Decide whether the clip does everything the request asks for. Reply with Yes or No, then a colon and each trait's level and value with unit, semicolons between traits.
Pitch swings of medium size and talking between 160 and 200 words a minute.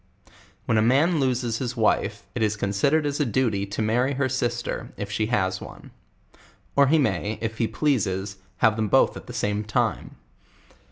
Yes: average, 3.8 semitones; average, 180 wpm